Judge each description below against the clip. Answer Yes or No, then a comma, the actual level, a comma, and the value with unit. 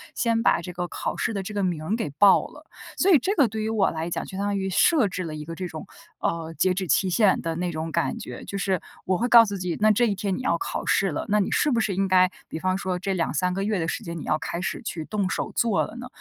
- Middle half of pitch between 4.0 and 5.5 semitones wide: No, average, 3.6 semitones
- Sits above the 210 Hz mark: No, high, 190 Hz